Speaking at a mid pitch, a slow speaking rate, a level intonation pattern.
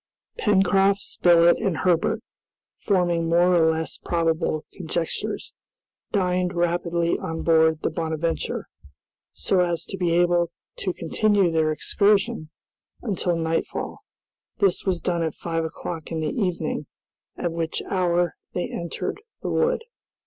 Yes: medium, 170 Hz; slow, 125 wpm; narrow, 2.0 semitones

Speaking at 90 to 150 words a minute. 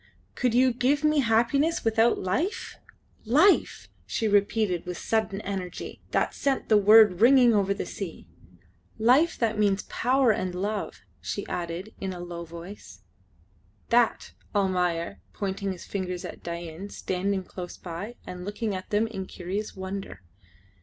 Yes: average, 145 wpm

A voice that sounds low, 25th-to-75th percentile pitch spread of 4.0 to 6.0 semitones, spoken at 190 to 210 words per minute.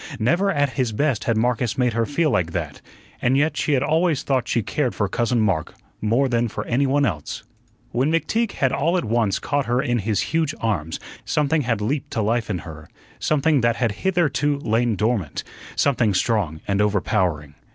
Yes: low, 120 Hz; average, 5.2 semitones; average, 195 wpm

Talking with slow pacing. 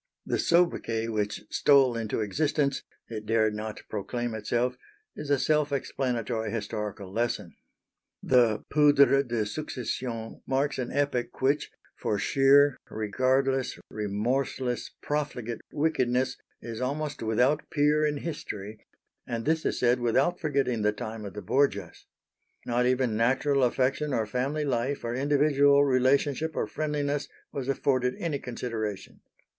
Yes: slow, 130 wpm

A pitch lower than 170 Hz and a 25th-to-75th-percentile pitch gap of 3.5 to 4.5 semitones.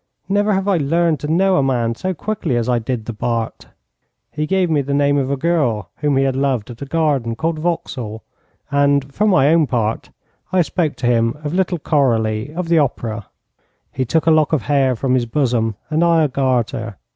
No: medium, 140 Hz; average, 5.3 semitones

